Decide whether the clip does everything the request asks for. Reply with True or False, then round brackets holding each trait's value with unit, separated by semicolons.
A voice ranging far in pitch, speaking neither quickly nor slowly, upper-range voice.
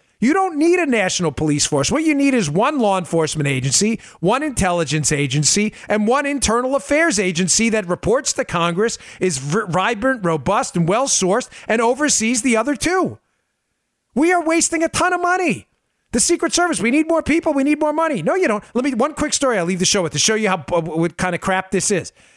False (8.1 semitones; 210 wpm; 225 Hz)